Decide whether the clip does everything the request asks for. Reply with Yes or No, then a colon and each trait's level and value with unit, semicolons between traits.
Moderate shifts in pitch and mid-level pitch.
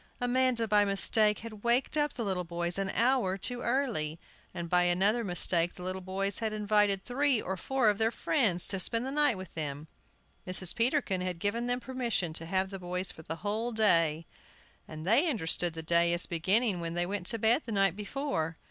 No: average, 5.0 semitones; high, 200 Hz